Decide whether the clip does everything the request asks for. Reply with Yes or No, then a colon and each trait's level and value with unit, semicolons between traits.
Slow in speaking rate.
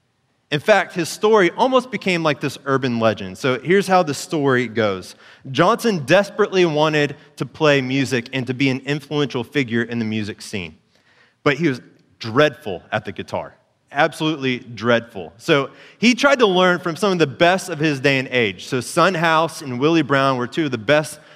No: average, 190 wpm